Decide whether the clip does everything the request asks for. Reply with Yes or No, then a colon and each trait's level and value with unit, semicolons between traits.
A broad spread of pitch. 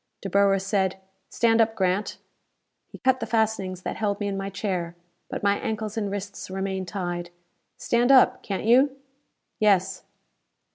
No: narrow, 2.5 semitones